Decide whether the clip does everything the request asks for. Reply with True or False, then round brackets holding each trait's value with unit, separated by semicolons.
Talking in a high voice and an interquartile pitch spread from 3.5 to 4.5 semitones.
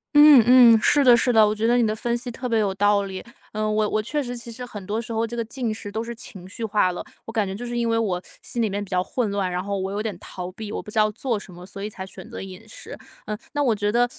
False (215 Hz; 2.8 semitones)